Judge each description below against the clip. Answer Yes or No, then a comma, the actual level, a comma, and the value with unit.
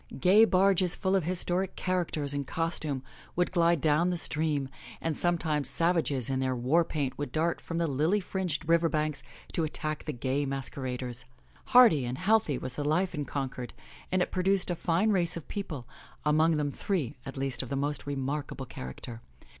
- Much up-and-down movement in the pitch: No, average, 4.4 semitones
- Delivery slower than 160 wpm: No, average, 180 wpm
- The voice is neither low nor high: Yes, medium, 155 Hz